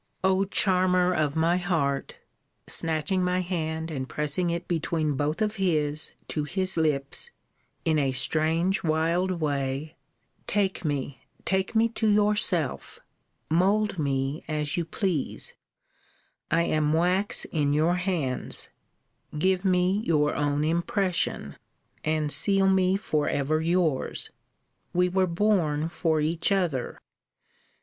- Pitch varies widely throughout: No, average, 3.7 semitones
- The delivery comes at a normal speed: No, slow, 125 wpm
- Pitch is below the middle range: No, medium, 165 Hz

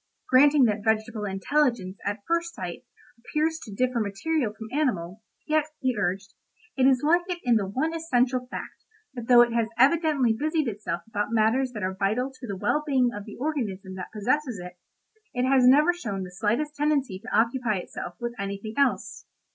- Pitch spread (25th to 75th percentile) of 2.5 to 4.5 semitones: No, wide, 5.5 semitones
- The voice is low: No, high, 240 Hz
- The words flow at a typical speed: Yes, average, 185 wpm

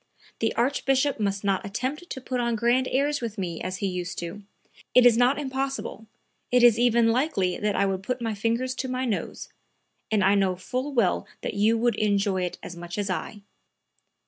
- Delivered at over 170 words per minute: Yes, average, 200 wpm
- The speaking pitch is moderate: No, high, 225 Hz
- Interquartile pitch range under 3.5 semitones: No, average, 4.4 semitones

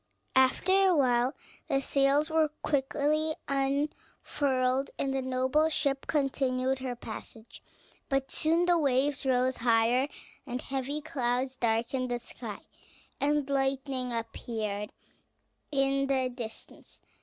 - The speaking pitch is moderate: No, very high, 270 Hz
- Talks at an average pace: No, slow, 110 wpm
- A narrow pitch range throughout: Yes, narrow, 2.0 semitones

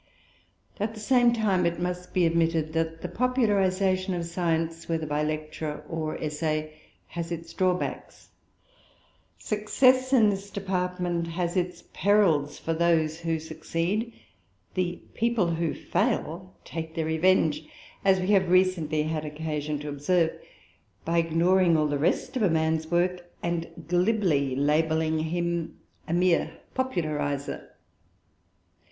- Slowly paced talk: Yes, slow, 130 wpm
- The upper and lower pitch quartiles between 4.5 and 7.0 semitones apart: No, average, 2.7 semitones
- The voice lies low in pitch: No, medium, 170 Hz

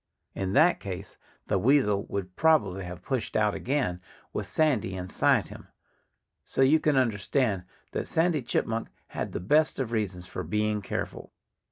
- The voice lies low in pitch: Yes, low, 105 Hz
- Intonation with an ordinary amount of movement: No, wide, 6.3 semitones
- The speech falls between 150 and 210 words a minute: Yes, average, 155 wpm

